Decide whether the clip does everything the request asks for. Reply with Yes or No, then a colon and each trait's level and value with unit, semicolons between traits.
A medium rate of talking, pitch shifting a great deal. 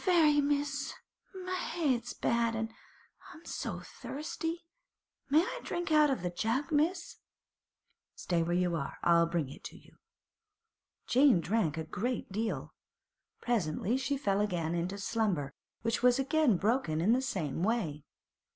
Yes: average, 150 wpm; wide, 8.7 semitones